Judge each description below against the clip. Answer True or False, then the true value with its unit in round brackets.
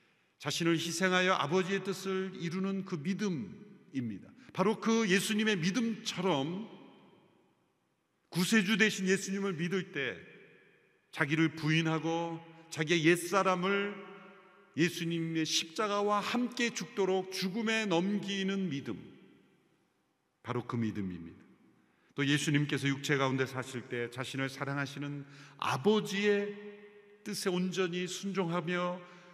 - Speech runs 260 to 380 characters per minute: False (250 characters per minute)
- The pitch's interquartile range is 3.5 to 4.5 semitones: True (4.0 semitones)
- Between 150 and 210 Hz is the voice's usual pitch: True (185 Hz)